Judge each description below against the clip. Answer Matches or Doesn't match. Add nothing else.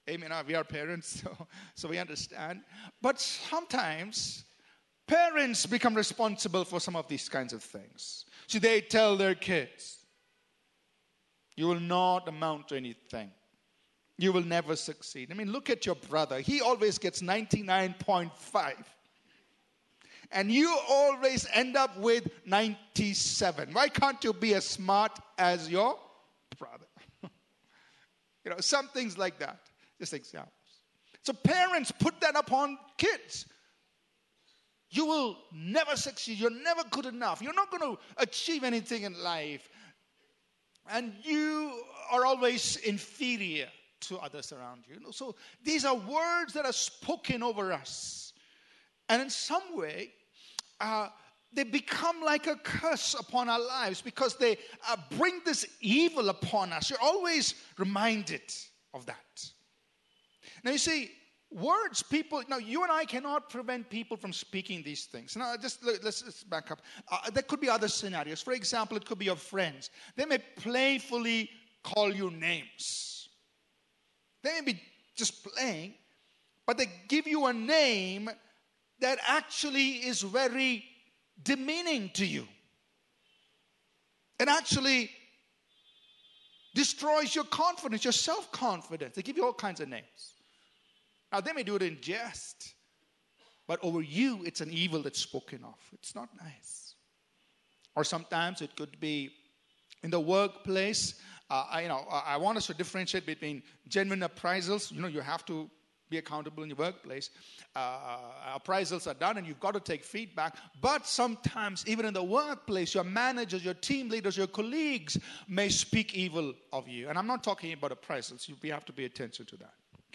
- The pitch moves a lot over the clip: Matches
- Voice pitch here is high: Matches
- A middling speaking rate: Matches